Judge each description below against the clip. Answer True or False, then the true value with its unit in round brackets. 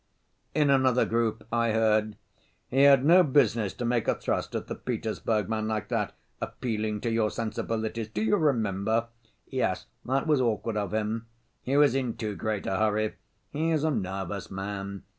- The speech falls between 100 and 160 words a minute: False (170 wpm)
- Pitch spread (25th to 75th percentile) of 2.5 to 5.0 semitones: True (3.4 semitones)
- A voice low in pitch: True (115 Hz)